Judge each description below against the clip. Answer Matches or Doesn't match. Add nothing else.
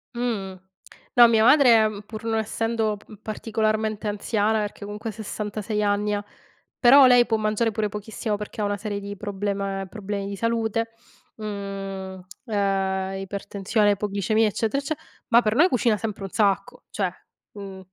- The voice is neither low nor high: Doesn't match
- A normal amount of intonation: Doesn't match